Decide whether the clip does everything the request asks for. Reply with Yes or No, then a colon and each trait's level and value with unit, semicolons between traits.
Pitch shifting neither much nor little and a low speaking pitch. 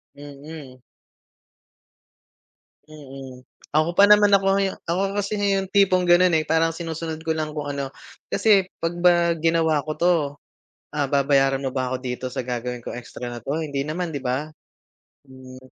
No: average, 4.3 semitones; medium, 155 Hz